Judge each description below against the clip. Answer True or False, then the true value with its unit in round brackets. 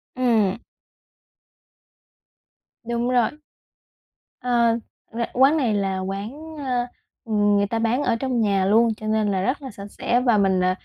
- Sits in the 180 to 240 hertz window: True (230 Hz)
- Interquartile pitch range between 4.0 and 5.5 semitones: False (3.6 semitones)